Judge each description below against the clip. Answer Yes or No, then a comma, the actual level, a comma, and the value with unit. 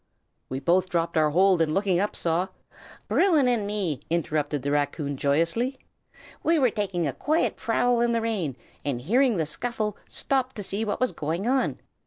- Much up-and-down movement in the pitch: Yes, wide, 7.1 semitones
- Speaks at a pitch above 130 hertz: Yes, high, 190 Hz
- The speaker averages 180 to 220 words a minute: Yes, average, 185 wpm